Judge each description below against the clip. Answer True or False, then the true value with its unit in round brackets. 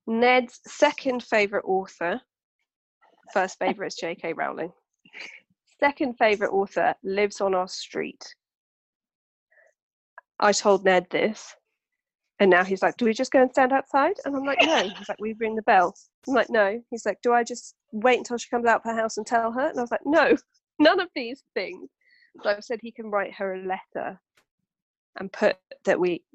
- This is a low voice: False (235 Hz)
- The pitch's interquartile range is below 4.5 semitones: False (5.1 semitones)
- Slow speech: False (185 wpm)